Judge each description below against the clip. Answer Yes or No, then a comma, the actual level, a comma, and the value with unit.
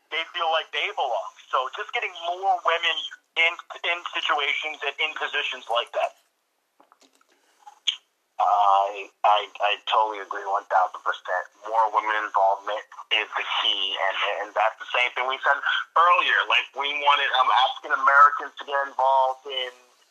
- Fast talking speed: No, average, 150 wpm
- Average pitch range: No, wide, 7.6 semitones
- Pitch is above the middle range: No, low, 135 Hz